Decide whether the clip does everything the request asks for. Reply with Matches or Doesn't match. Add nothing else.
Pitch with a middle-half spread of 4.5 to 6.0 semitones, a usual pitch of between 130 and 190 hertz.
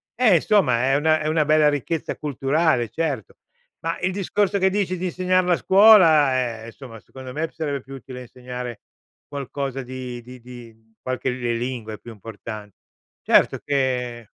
Matches